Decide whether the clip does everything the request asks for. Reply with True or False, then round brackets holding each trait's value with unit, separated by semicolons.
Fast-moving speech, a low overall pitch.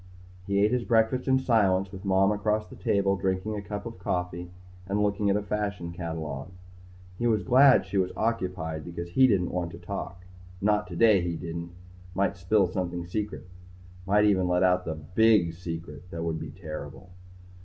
False (180 wpm; 95 Hz)